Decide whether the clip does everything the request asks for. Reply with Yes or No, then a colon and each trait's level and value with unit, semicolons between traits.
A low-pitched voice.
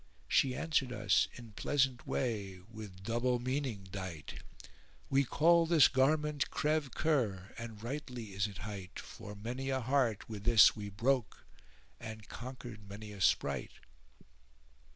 Yes: low, 115 Hz